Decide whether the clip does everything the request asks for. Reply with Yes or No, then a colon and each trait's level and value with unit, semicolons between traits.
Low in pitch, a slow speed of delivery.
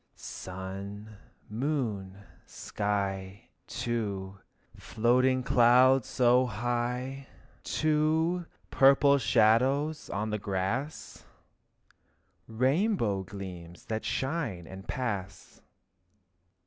Yes: low, 115 Hz; slow, 80 wpm